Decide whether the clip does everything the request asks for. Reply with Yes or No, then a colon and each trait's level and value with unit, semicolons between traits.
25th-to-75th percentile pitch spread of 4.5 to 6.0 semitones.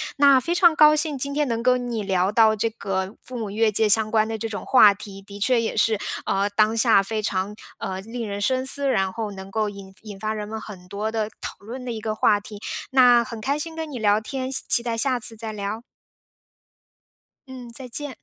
No: average, 3.5 semitones